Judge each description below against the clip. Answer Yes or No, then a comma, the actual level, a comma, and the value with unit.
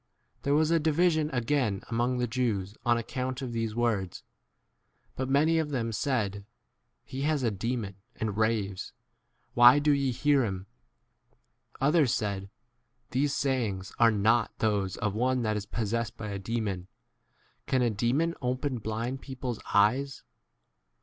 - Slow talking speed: No, average, 160 wpm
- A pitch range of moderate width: Yes, average, 4.1 semitones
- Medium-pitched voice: No, low, 120 Hz